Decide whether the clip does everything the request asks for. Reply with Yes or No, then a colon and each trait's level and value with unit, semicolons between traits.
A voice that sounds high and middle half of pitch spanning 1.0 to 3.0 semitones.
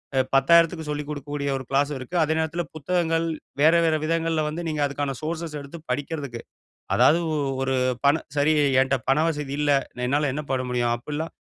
No: medium, 150 Hz; average, 2.7 semitones